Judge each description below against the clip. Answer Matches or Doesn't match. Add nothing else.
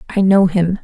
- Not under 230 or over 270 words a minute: Doesn't match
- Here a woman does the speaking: Matches